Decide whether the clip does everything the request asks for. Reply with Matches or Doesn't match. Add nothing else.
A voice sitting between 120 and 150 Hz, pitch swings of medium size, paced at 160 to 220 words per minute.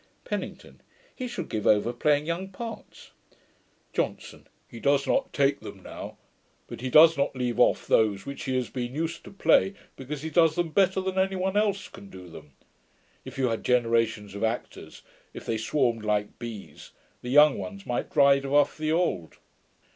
Doesn't match